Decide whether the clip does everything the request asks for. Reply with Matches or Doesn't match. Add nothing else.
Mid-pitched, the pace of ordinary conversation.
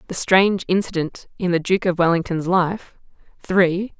Matches